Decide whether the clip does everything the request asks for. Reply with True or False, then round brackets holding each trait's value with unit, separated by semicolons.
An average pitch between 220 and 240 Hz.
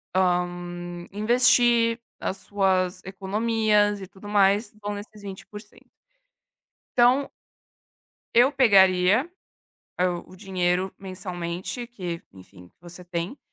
False (195 Hz)